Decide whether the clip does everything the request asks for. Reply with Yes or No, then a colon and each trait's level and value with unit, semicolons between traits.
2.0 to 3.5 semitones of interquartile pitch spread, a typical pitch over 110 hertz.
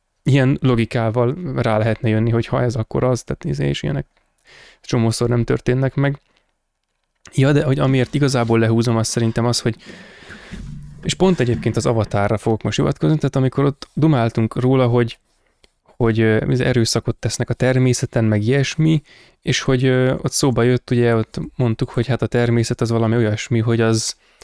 Yes: average, 2.8 semitones; low, 120 Hz